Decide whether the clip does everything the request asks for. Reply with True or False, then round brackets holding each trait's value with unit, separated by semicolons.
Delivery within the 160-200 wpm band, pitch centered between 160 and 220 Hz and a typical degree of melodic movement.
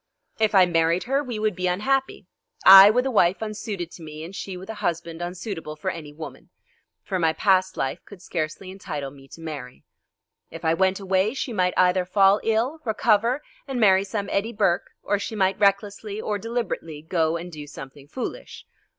True (190 wpm; 190 Hz; 4.3 semitones)